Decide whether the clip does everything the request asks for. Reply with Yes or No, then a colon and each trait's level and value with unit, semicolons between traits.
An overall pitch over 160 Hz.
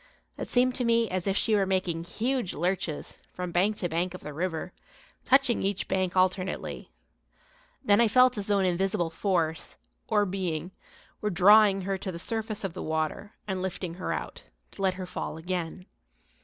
Yes: high, 190 Hz